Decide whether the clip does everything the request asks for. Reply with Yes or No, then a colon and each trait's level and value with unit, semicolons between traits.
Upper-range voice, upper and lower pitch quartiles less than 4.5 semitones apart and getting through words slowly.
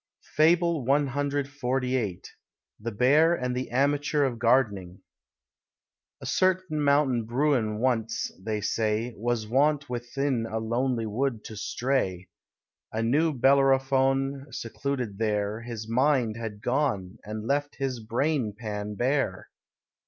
No: low, 125 Hz; average, 4.0 semitones; slow, 115 wpm